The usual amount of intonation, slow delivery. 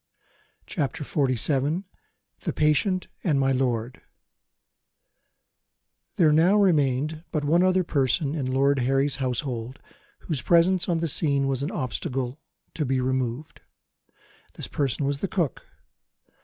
Yes: average, 3.6 semitones; slow, 125 wpm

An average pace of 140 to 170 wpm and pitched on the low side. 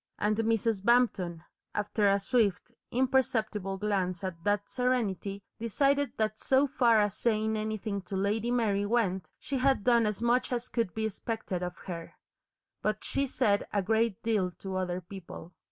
No: average, 160 wpm; high, 215 Hz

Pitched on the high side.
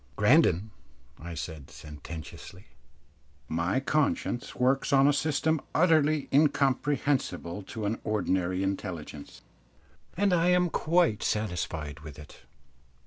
No: low, 110 Hz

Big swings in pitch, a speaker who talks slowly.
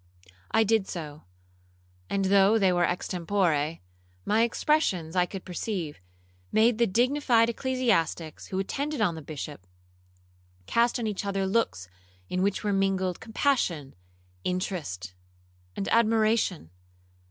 No: average, 4.8 semitones; slow, 120 wpm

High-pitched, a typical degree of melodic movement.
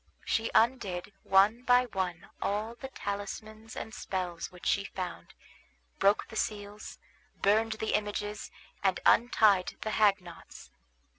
No: high, 205 Hz; narrow, 2.3 semitones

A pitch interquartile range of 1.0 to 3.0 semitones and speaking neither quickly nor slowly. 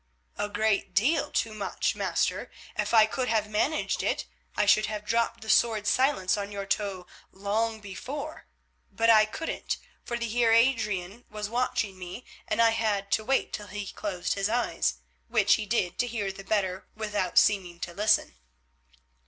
Yes: narrow, 2.5 semitones; average, 170 wpm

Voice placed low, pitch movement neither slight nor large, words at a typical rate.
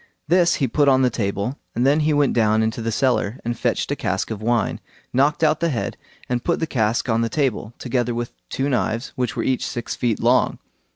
No: low, 125 Hz; average, 3.5 semitones; fast, 225 wpm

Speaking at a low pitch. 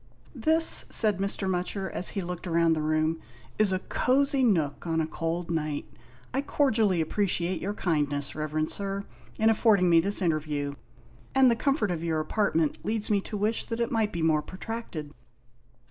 No: medium, 185 Hz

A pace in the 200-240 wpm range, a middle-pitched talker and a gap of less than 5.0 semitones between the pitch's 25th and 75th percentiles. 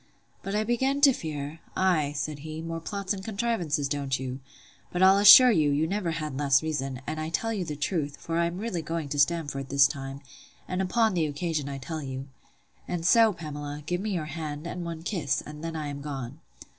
Yes: fast, 205 wpm; medium, 160 Hz; average, 4.1 semitones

